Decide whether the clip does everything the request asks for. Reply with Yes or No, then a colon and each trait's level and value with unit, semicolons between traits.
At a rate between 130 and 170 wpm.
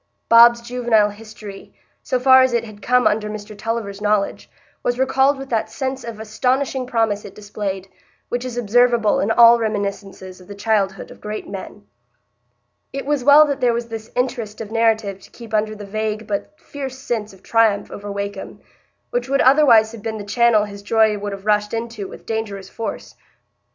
No: average, 185 wpm